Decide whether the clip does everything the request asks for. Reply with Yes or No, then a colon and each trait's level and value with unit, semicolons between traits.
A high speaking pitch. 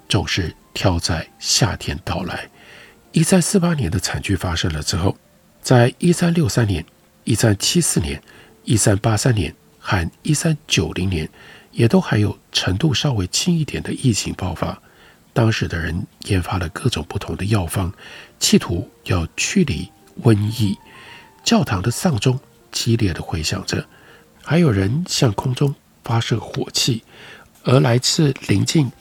No: low, 110 Hz